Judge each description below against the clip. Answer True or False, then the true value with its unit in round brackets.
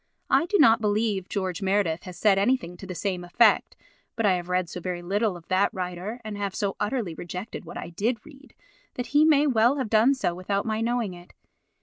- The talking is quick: True (220 wpm)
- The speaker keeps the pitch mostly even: False (4.2 semitones)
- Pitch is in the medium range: False (205 Hz)